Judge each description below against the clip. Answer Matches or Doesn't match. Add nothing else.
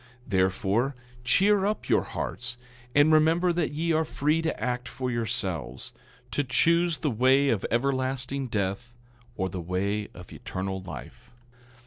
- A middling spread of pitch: Doesn't match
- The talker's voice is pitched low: Matches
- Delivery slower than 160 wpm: Matches